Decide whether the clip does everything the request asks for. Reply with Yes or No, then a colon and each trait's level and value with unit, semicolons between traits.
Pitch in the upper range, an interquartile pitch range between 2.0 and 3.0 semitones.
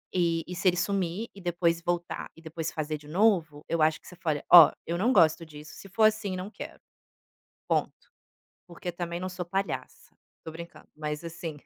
No: medium, 170 Hz; narrow, 2.4 semitones